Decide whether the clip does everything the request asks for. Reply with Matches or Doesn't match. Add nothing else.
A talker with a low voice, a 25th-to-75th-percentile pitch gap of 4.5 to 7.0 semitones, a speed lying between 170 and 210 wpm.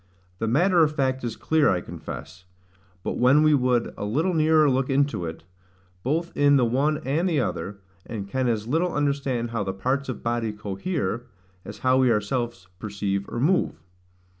Matches